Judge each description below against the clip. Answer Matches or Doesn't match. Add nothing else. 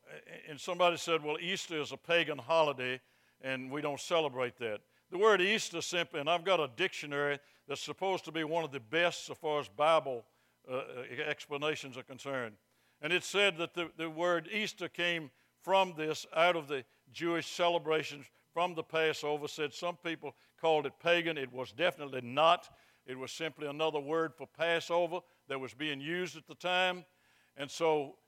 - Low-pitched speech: Doesn't match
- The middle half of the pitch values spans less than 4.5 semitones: Matches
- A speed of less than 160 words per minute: Doesn't match